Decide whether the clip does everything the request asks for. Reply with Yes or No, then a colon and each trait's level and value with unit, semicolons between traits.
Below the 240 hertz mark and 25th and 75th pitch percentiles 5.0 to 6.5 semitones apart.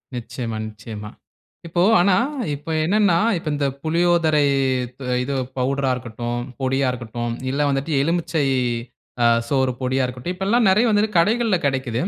Yes: medium, 140 Hz; wide, 5.6 semitones